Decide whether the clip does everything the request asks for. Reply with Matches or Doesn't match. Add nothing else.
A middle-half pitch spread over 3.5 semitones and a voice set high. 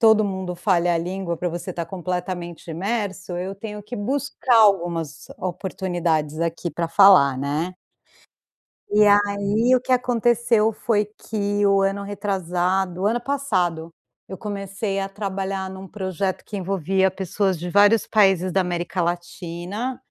Doesn't match